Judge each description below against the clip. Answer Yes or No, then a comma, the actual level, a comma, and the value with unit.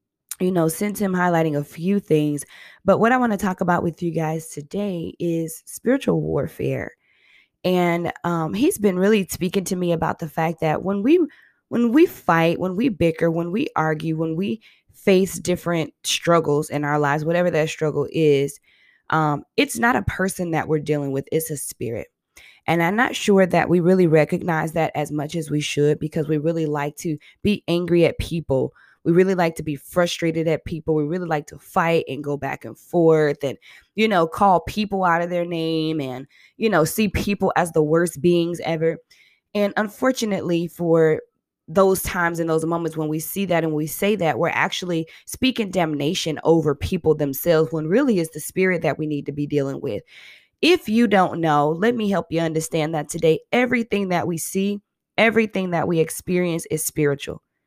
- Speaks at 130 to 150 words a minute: No, average, 195 wpm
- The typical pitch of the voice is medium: Yes, medium, 165 Hz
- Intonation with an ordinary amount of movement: Yes, average, 3.3 semitones